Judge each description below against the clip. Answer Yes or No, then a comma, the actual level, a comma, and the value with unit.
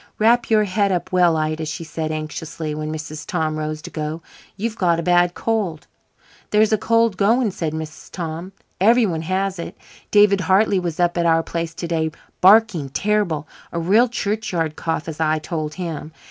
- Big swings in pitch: No, average, 4.4 semitones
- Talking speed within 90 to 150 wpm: No, average, 180 wpm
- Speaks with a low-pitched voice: No, medium, 170 Hz